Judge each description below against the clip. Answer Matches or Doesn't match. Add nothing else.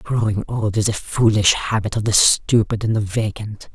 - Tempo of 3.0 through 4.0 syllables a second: Doesn't match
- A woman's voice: Matches